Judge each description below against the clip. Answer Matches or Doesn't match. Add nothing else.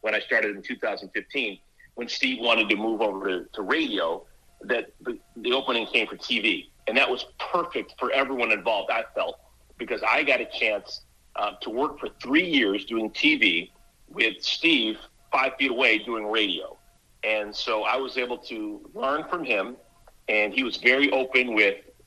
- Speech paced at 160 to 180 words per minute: Matches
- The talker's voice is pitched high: Doesn't match